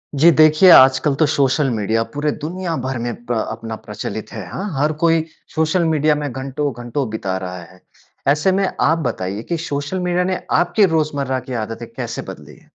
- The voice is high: No, medium, 140 Hz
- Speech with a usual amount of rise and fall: No, wide, 5.9 semitones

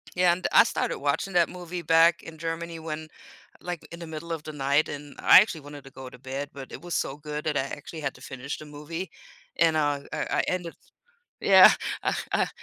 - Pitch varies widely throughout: No, average, 2.7 semitones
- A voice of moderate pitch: Yes, medium, 155 Hz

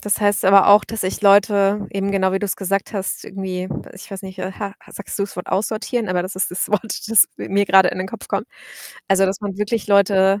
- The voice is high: Yes, high, 195 Hz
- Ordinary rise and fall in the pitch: No, narrow, 1.3 semitones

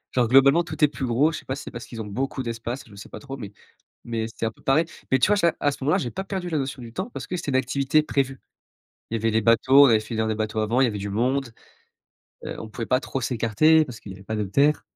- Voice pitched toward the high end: No, low, 125 Hz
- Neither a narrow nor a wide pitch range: Yes, average, 4.1 semitones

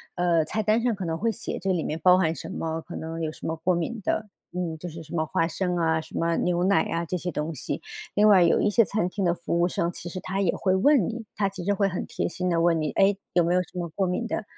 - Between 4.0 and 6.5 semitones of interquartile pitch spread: No, average, 2.8 semitones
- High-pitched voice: No, medium, 175 Hz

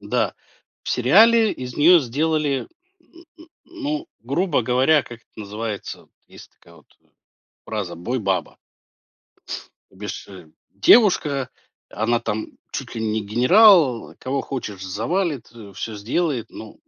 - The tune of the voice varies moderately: No, wide, 6.9 semitones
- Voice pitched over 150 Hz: No, low, 125 Hz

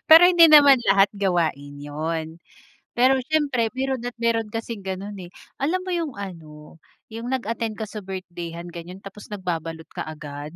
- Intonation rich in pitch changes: Yes, wide, 6.6 semitones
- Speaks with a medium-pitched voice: No, high, 195 Hz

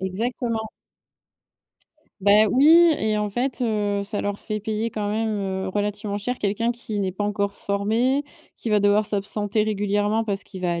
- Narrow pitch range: Yes, narrow, 1.8 semitones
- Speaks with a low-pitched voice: No, high, 210 Hz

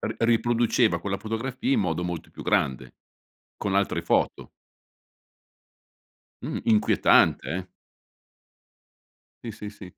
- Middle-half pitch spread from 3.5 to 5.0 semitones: Yes, average, 4.6 semitones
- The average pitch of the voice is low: Yes, low, 105 Hz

